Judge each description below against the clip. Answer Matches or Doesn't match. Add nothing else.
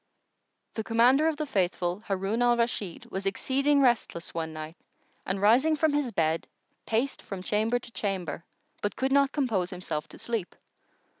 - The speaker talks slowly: Doesn't match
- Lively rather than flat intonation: Matches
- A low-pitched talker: Doesn't match